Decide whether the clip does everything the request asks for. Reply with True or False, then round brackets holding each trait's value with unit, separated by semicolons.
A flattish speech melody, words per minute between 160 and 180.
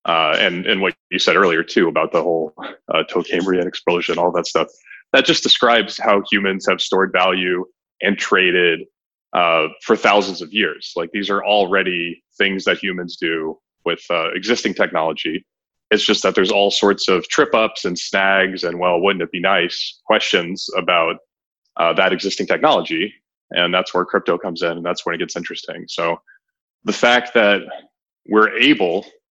True (2.1 semitones; 175 wpm)